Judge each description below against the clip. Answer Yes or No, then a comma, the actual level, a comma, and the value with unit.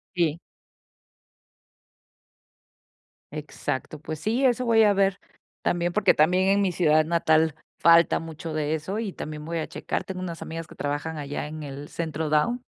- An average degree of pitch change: Yes, average, 3.5 semitones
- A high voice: No, medium, 165 Hz